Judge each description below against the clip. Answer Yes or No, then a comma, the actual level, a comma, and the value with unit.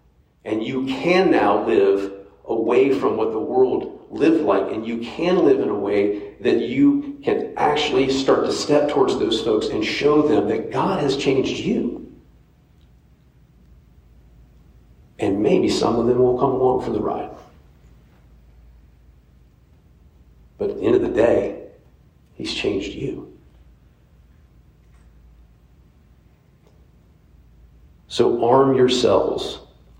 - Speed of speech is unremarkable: No, slow, 120 wpm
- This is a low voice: Yes, very low, 80 Hz